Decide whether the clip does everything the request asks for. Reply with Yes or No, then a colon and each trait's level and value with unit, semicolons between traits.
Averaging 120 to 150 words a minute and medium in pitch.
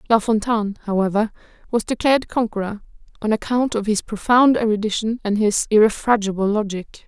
No: slow, 135 wpm; high, 215 Hz